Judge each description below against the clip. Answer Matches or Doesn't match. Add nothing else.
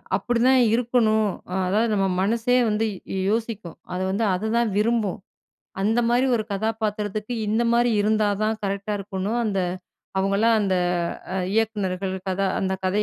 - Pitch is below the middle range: Doesn't match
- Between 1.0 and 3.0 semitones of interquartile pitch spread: Matches